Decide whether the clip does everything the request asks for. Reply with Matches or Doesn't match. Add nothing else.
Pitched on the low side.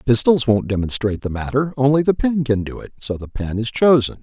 Matches